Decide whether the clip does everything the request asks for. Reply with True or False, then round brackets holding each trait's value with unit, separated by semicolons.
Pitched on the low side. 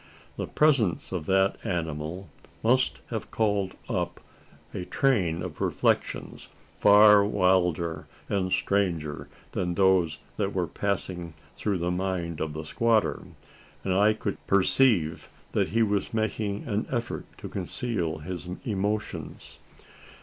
True (95 Hz)